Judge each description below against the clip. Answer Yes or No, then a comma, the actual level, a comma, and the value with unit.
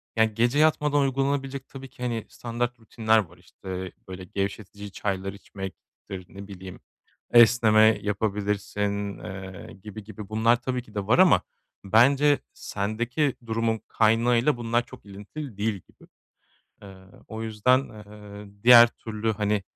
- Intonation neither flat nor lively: Yes, average, 3.1 semitones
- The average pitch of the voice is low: Yes, low, 110 Hz